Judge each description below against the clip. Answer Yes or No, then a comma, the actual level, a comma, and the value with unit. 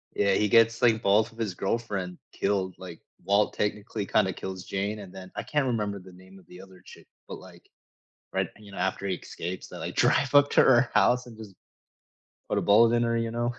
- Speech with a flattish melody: No, average, 3.3 semitones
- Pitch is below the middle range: Yes, low, 105 Hz